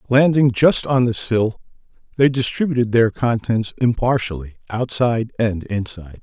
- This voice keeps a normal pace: No, slow, 125 wpm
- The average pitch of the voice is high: No, low, 115 Hz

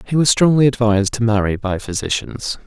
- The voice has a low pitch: Yes, low, 115 Hz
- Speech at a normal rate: Yes, average, 180 wpm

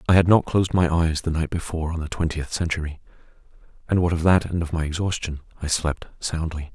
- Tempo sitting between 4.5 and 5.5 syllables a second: No, 6.1 syllables/s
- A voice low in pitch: Yes, very low, 80 Hz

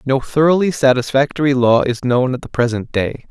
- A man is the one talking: Yes, male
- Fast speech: No, average, 180 wpm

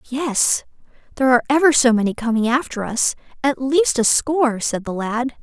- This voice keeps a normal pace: Yes, average, 175 wpm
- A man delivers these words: No, female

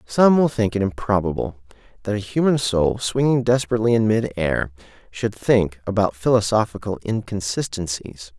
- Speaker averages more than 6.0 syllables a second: No, 5.1 syllables/s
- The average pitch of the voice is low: Yes, low, 105 Hz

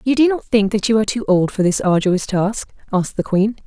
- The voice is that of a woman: Yes, female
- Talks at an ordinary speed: No, fast, 260 wpm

